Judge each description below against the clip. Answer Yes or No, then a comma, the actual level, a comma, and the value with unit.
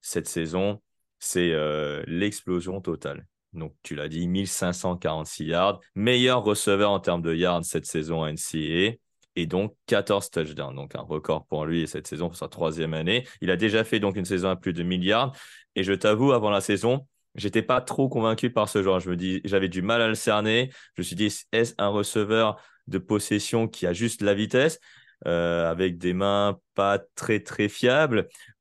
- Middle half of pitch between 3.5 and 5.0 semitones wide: Yes, average, 4.0 semitones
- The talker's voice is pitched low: Yes, very low, 95 Hz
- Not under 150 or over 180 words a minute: No, average, 195 wpm